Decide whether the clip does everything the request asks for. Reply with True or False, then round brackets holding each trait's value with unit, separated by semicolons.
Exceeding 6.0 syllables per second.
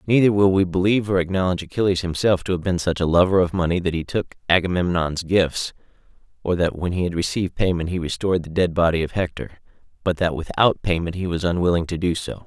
True (6.3 syllables/s)